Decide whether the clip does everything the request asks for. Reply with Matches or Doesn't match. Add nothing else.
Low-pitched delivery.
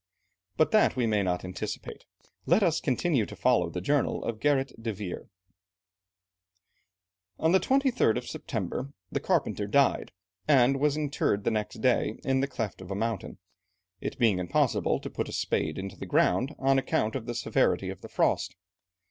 Matches